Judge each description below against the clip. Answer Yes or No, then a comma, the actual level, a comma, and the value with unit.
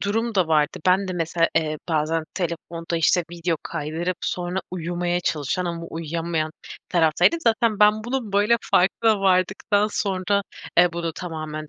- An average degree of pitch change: Yes, average, 3.3 semitones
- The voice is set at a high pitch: No, medium, 175 Hz